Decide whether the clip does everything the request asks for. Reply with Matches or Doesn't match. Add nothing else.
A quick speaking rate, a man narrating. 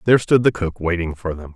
Matches